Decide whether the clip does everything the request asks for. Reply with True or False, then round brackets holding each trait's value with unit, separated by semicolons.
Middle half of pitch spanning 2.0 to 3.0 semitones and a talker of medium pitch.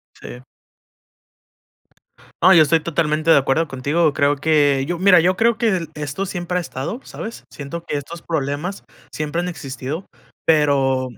False (3.6 semitones; 155 Hz)